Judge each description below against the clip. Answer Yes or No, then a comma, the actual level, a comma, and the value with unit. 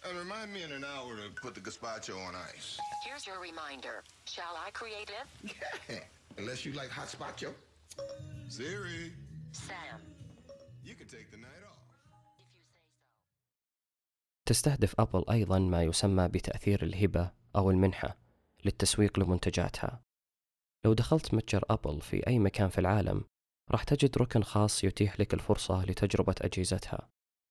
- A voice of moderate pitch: No, low, 105 Hz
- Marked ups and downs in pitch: Yes, wide, 6.1 semitones